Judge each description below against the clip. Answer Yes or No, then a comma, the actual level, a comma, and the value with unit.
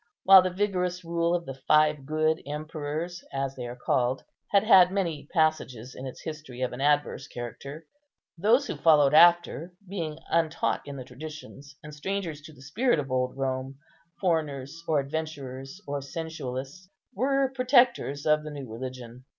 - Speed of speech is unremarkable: Yes, average, 160 wpm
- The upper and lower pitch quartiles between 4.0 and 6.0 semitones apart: Yes, average, 4.3 semitones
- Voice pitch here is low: No, medium, 155 Hz